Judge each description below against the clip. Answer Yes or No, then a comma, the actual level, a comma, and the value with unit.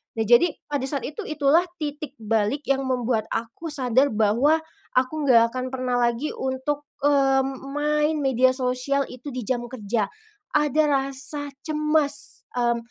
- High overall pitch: Yes, very high, 265 Hz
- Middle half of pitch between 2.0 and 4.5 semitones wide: Yes, average, 3.1 semitones